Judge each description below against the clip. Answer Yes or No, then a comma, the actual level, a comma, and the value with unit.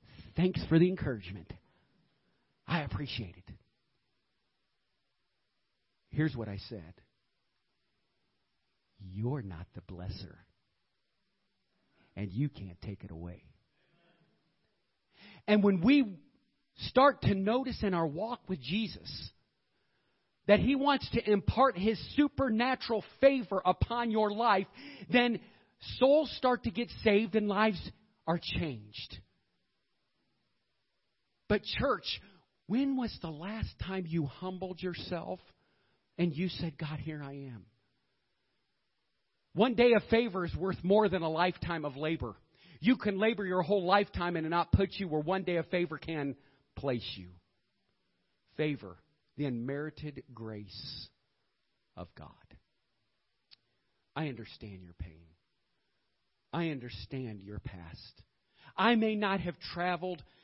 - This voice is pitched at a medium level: Yes, medium, 165 Hz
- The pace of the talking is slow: Yes, slow, 120 wpm